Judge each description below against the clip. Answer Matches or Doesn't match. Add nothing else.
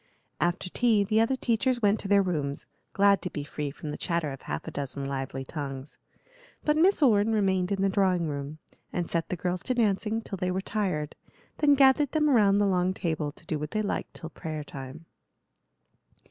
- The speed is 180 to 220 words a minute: Matches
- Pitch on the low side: Doesn't match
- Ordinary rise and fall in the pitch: Doesn't match